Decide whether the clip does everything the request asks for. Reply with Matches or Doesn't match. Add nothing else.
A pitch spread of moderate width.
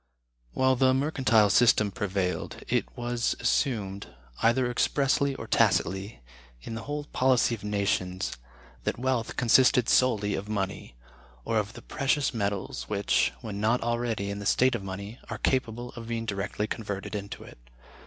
Matches